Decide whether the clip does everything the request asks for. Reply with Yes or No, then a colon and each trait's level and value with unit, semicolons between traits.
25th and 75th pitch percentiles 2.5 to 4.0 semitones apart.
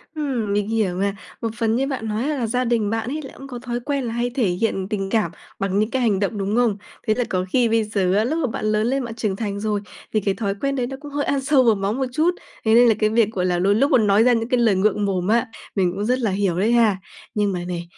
Yes: average, 3.5 semitones